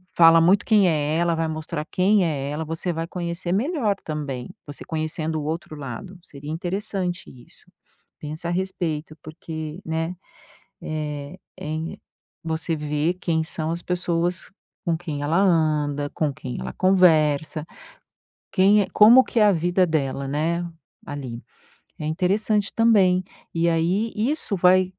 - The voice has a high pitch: No, medium, 165 Hz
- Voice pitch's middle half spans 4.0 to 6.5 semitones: No, average, 3.2 semitones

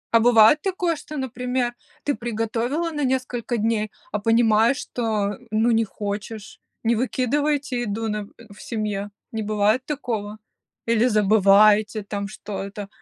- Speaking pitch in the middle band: No, high, 225 Hz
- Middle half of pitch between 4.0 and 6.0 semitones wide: No, average, 2.9 semitones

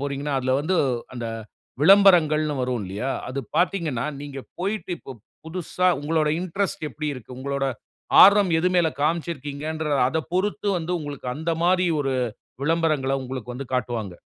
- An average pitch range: Yes, average, 4.4 semitones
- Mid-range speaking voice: Yes, medium, 150 Hz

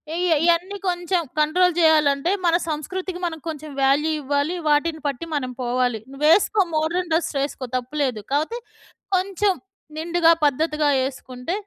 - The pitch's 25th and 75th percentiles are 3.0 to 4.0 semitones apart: Yes, average, 3.6 semitones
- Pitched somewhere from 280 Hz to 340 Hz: Yes, very high, 315 Hz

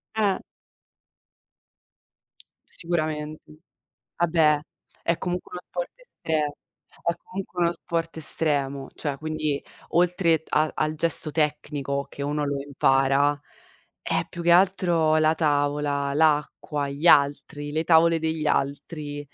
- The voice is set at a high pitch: No, medium, 155 Hz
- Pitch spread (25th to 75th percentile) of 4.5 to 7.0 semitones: No, narrow, 2.5 semitones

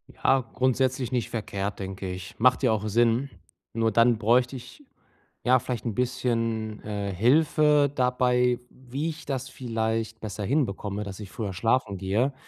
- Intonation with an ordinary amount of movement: Yes, average, 3.3 semitones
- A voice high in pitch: No, low, 115 Hz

